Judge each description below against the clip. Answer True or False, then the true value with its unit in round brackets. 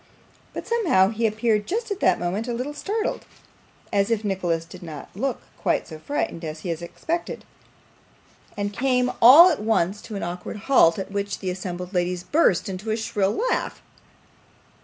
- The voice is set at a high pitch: True (205 Hz)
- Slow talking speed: False (175 wpm)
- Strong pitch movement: True (5.7 semitones)